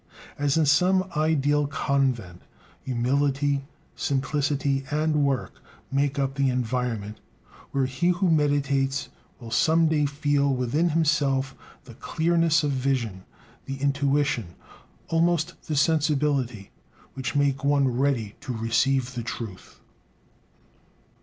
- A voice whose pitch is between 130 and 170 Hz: Yes, medium, 140 Hz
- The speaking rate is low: Yes, slow, 115 wpm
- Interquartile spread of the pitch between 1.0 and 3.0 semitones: Yes, narrow, 2.4 semitones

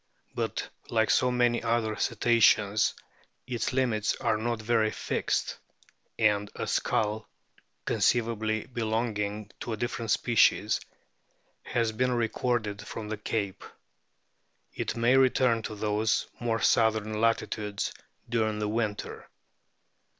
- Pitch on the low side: Yes, low, 110 Hz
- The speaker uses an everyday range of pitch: No, narrow, 1.9 semitones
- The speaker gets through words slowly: Yes, slow, 115 wpm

